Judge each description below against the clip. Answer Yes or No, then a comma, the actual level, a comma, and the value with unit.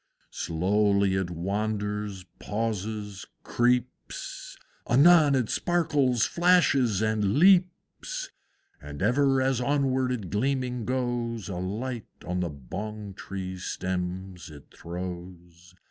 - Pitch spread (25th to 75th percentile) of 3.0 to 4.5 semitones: No, wide, 5.5 semitones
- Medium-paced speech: No, slow, 100 wpm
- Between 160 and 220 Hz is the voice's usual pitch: No, low, 105 Hz